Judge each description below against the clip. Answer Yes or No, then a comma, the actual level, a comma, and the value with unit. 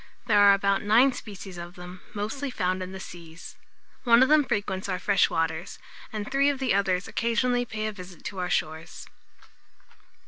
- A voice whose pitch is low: No, high, 200 Hz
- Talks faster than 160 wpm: Yes, average, 180 wpm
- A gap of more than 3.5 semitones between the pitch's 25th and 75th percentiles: Yes, average, 4.4 semitones